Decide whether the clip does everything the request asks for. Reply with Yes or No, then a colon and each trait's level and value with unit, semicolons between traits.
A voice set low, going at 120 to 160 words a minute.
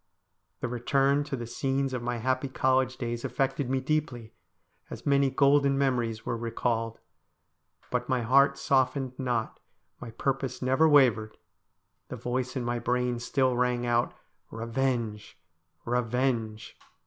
Yes: low, 125 Hz; average, 140 wpm